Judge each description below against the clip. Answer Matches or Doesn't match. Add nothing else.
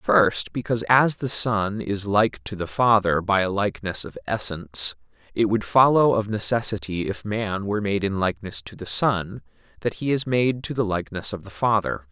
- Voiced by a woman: Doesn't match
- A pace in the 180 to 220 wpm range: Matches